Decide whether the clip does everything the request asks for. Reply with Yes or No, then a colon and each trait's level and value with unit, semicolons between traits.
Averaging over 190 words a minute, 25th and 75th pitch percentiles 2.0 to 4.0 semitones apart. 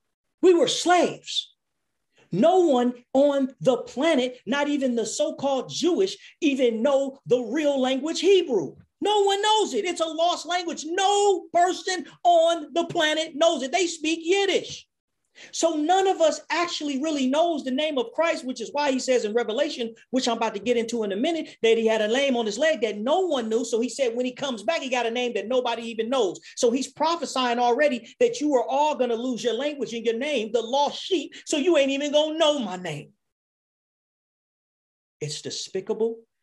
No: average, 200 wpm; average, 5.3 semitones